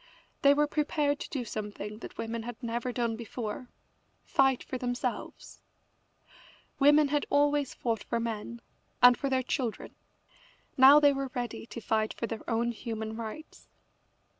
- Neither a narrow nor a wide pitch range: Yes, average, 3.6 semitones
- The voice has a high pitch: Yes, high, 245 Hz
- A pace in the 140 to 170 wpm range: Yes, average, 150 wpm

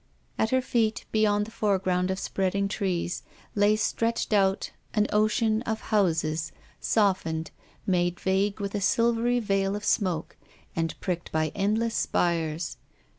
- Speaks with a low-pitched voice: No, high, 200 Hz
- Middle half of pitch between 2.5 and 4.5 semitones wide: Yes, average, 3.3 semitones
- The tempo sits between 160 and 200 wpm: No, average, 145 wpm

